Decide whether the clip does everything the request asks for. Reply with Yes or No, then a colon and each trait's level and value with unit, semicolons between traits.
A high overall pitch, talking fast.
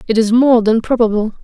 Yes: high, 225 Hz; fast, 210 wpm